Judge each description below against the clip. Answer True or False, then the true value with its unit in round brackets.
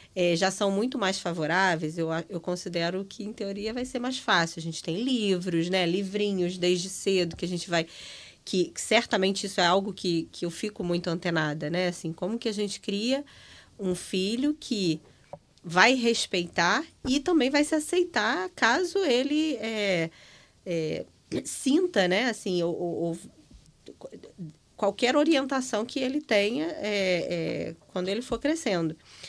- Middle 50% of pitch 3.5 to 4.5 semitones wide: False (5.1 semitones)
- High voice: True (195 Hz)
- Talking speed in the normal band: True (160 wpm)